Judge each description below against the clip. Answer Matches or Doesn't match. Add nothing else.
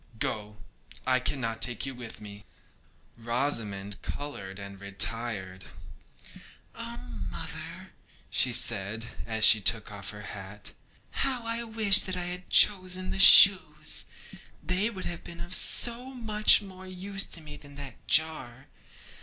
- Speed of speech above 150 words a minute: Doesn't match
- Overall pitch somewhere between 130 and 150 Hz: Matches